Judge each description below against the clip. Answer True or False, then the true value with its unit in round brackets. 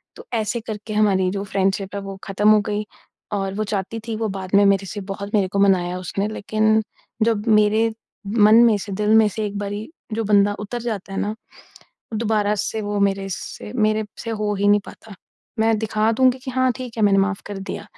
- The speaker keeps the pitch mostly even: True (1.6 semitones)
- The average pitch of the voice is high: True (210 Hz)